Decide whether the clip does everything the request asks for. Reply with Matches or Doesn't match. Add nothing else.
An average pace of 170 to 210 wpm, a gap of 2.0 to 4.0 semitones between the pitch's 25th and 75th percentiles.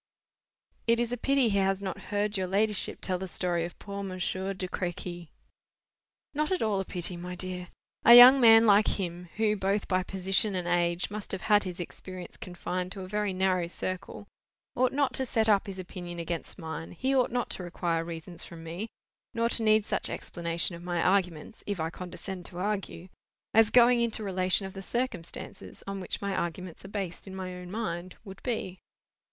Matches